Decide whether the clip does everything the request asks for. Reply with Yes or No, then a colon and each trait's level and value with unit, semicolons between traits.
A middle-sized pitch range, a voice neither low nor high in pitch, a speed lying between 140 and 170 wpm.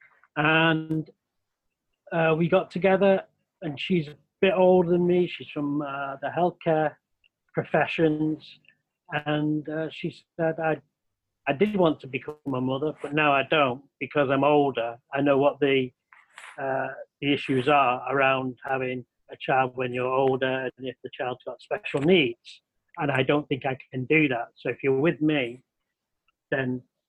Yes: average, 3.3 semitones; medium, 145 Hz; average, 160 wpm